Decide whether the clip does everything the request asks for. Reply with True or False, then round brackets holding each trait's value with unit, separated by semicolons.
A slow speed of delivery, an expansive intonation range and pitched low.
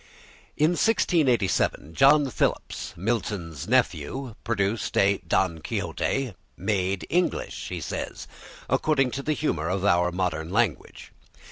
True (115 wpm; 7.4 semitones; 100 Hz)